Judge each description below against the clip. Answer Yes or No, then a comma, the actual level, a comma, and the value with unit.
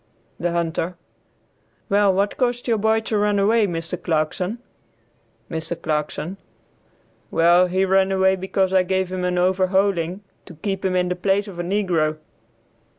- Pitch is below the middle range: No, medium, 185 Hz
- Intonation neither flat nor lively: No, narrow, 2.3 semitones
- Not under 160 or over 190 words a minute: No, average, 150 wpm